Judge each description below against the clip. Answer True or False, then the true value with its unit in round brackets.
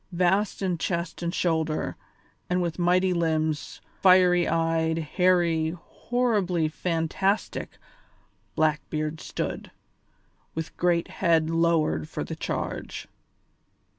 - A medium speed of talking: False (100 wpm)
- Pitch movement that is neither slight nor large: False (2.1 semitones)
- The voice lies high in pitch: False (170 Hz)